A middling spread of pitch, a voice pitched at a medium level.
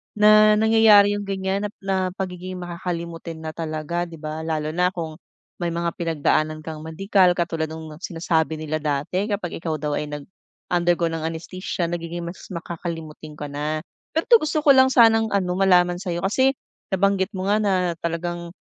Yes: average, 3.4 semitones; medium, 175 Hz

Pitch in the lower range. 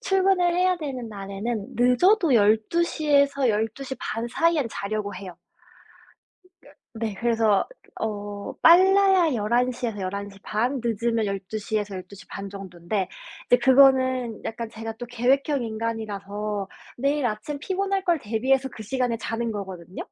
No: high, 230 Hz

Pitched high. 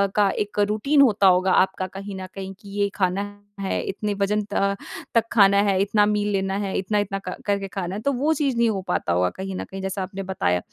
Yes: high, 195 Hz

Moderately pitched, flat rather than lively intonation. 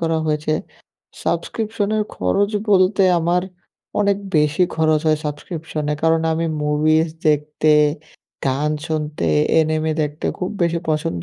Yes: medium, 155 Hz; narrow, 2.1 semitones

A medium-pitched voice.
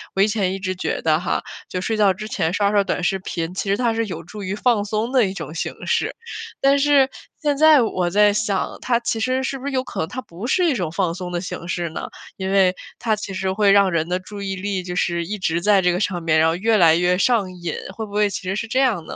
No: high, 195 Hz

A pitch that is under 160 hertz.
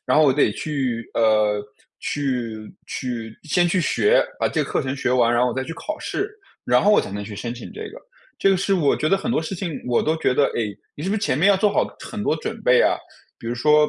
Yes: medium, 140 Hz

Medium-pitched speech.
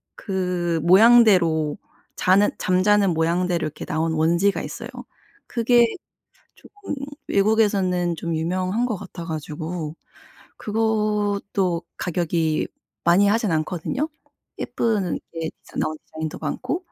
Yes: medium, 180 Hz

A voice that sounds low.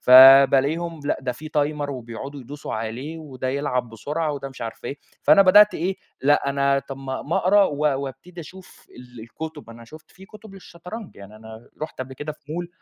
No: medium, 145 Hz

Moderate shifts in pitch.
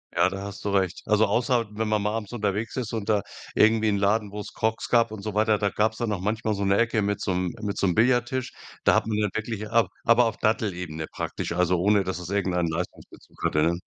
No: narrow, 2.3 semitones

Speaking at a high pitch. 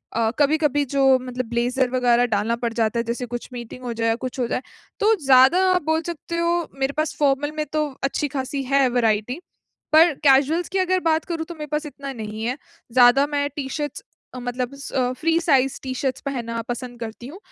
Yes: very high, 265 Hz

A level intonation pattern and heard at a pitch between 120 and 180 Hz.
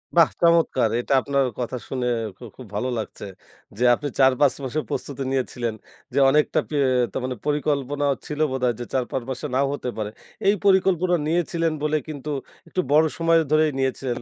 No: average, 3.5 semitones; medium, 140 Hz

